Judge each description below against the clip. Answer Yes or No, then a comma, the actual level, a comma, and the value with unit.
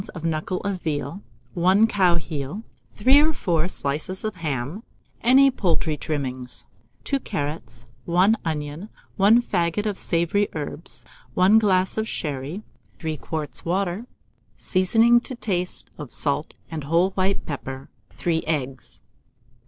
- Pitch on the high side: No, medium, 175 Hz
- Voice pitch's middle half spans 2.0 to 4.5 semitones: No, average, 5.0 semitones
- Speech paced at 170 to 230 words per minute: No, slow, 135 wpm